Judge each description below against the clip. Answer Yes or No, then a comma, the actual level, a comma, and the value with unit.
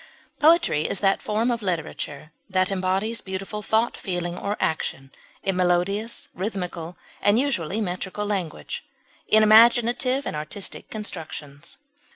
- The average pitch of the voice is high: Yes, high, 195 Hz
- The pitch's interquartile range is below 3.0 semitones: No, average, 3.8 semitones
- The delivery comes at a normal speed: No, slow, 125 wpm